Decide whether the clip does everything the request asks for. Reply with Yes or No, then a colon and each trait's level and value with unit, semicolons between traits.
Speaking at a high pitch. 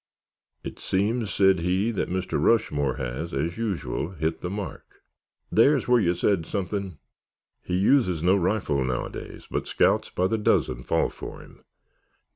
No: very low, 95 Hz